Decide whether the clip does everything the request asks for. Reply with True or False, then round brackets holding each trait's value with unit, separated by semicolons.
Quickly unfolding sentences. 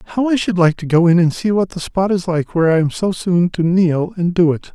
True (305 wpm)